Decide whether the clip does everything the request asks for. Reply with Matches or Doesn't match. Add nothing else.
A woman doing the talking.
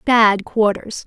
Matches